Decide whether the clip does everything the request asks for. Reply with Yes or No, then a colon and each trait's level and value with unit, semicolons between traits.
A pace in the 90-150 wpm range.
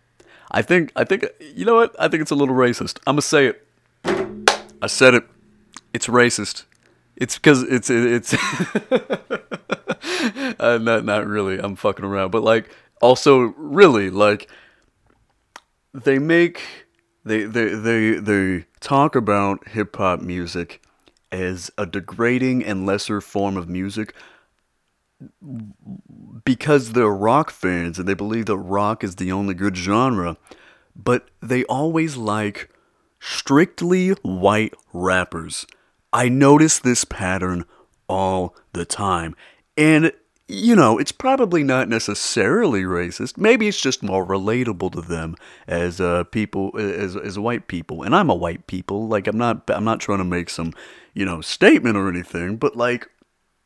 Yes: average, 145 wpm